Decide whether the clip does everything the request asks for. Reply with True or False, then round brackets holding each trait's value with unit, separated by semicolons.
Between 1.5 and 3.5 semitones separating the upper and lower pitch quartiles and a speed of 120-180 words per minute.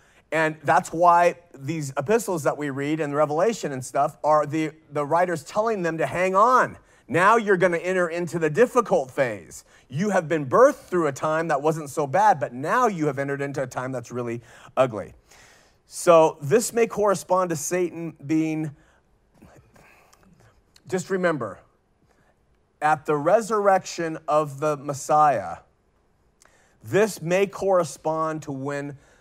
False (3.9 semitones; 145 wpm)